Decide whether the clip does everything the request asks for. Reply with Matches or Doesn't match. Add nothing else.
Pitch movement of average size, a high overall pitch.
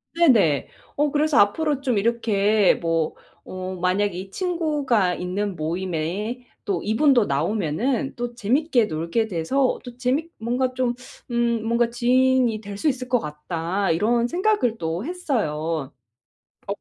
Doesn't match